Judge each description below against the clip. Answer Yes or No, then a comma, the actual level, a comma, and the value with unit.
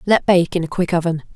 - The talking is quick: Yes, fast, 265 wpm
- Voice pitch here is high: No, medium, 175 Hz